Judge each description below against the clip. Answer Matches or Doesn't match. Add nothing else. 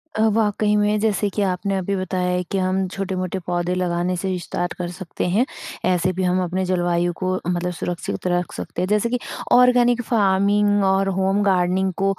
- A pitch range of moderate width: Doesn't match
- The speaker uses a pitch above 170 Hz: Matches